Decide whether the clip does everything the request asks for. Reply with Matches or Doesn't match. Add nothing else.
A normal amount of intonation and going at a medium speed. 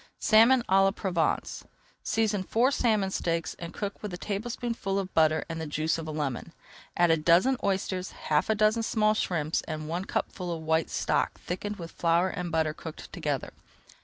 Matches